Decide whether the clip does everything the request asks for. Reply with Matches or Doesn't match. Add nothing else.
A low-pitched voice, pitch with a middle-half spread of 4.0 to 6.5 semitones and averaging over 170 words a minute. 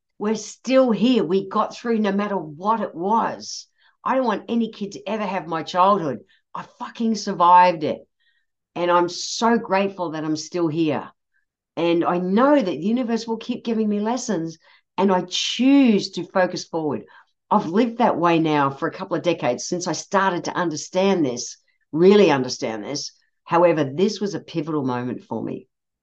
Doesn't match